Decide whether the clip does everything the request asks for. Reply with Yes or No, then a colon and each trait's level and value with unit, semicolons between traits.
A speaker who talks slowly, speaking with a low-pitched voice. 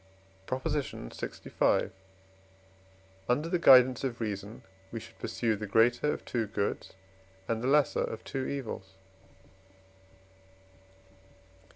Yes: slow, 105 wpm; low, 120 Hz